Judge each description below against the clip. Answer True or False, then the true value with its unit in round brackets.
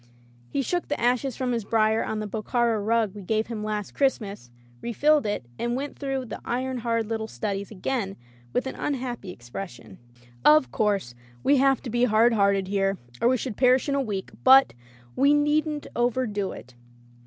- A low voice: False (230 Hz)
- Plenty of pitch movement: False (4.4 semitones)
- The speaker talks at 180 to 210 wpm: True (190 wpm)